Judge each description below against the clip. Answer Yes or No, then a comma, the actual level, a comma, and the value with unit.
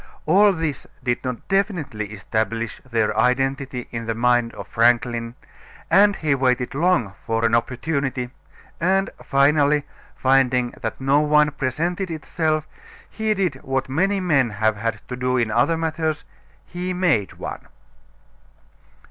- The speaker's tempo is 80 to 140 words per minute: Yes, slow, 135 wpm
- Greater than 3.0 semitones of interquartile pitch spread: Yes, wide, 5.4 semitones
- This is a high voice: No, low, 135 Hz